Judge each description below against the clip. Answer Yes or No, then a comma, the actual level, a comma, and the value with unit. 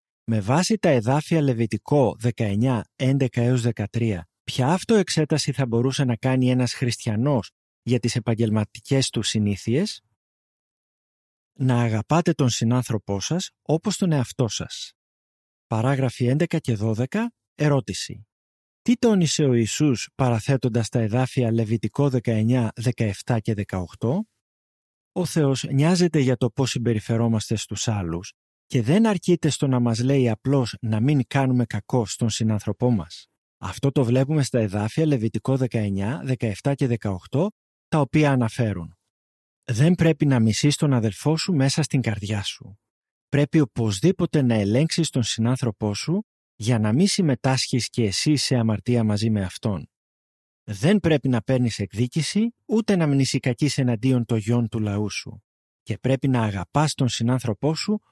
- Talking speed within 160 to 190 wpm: No, average, 135 wpm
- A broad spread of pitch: No, average, 4.4 semitones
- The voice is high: No, low, 125 Hz